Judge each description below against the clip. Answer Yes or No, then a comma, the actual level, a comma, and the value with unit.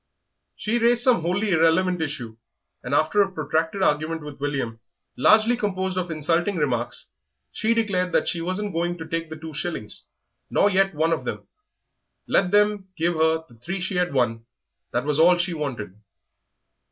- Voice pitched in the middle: Yes, medium, 165 Hz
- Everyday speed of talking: Yes, average, 170 wpm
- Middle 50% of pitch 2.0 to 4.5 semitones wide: Yes, average, 4.1 semitones